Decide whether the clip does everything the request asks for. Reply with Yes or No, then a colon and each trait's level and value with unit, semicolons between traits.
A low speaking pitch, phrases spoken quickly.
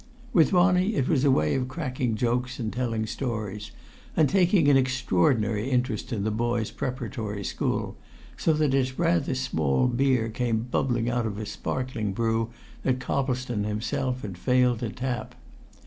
No: low, 125 Hz; average, 160 wpm